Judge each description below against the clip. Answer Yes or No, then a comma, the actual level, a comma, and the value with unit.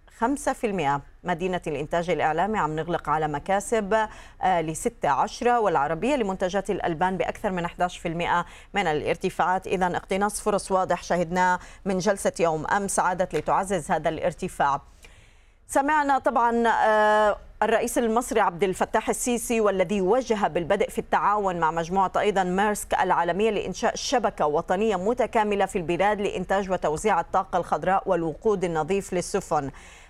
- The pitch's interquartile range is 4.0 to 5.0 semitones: No, average, 3.5 semitones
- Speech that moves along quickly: No, average, 120 wpm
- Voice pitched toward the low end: No, high, 195 Hz